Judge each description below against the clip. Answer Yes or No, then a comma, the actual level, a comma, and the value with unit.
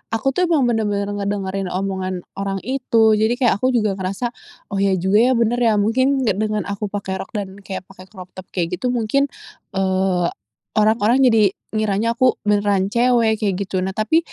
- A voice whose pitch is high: Yes, high, 210 Hz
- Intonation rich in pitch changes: No, average, 3.3 semitones